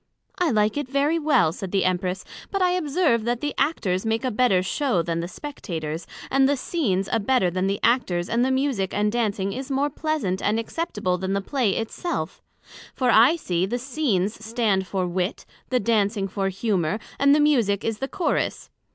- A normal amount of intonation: No, wide, 6.3 semitones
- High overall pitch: Yes, high, 220 Hz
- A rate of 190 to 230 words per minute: Yes, average, 195 wpm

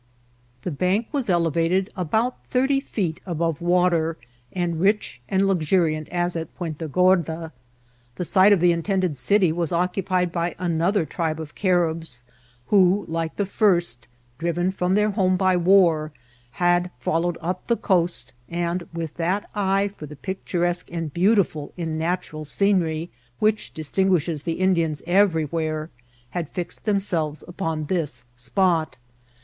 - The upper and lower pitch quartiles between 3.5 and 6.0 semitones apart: No, average, 2.8 semitones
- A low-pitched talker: No, medium, 175 Hz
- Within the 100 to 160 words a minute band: Yes, average, 140 wpm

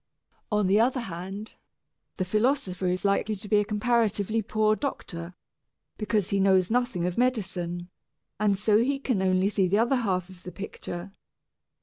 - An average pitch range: Yes, average, 3.2 semitones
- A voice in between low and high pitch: No, high, 205 Hz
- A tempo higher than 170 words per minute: No, average, 155 wpm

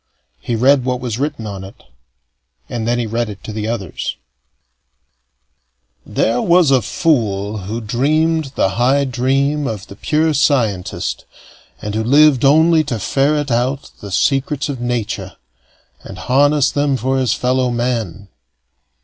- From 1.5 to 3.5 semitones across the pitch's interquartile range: No, average, 4.2 semitones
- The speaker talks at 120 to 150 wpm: Yes, average, 145 wpm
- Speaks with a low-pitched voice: Yes, low, 125 Hz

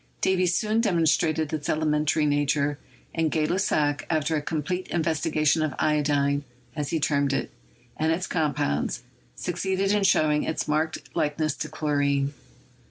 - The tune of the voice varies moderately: No, narrow, 2.0 semitones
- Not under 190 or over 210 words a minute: No, average, 145 wpm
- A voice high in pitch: No, medium, 155 Hz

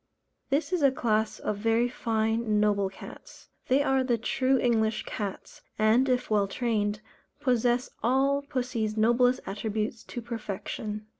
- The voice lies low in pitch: No, high, 230 Hz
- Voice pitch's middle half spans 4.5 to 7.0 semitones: No, average, 2.9 semitones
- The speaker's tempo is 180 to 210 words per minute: No, average, 140 wpm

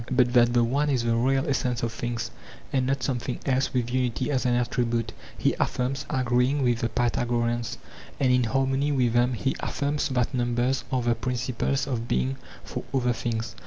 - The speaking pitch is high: No, low, 125 Hz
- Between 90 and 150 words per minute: No, average, 185 wpm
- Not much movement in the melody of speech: Yes, narrow, 1.9 semitones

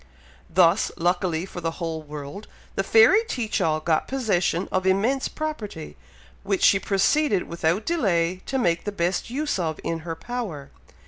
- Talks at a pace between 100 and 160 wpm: Yes, average, 155 wpm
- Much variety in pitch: No, average, 5.0 semitones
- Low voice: No, medium, 185 Hz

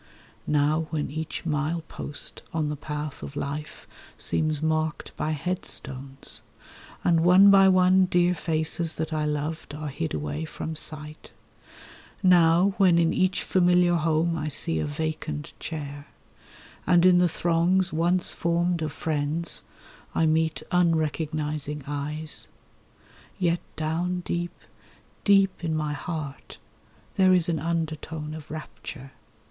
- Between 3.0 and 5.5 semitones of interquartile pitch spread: No, narrow, 2.5 semitones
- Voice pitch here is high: No, medium, 160 Hz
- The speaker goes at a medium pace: No, slow, 130 wpm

